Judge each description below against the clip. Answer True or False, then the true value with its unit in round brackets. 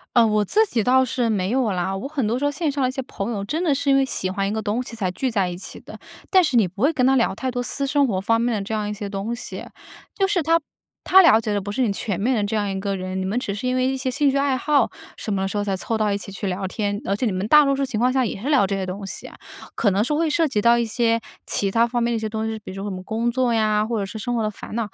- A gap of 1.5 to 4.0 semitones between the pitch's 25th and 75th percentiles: False (4.4 semitones)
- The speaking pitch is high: True (225 Hz)